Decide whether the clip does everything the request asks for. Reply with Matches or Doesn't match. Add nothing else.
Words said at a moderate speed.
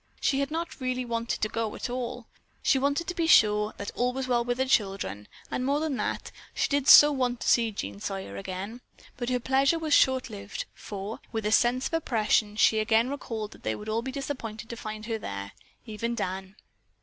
Doesn't match